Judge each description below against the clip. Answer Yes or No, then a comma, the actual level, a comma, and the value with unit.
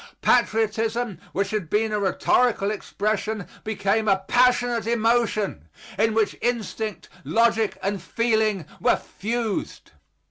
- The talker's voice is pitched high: Yes, high, 220 Hz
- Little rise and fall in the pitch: Yes, narrow, 2.3 semitones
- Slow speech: Yes, slow, 110 wpm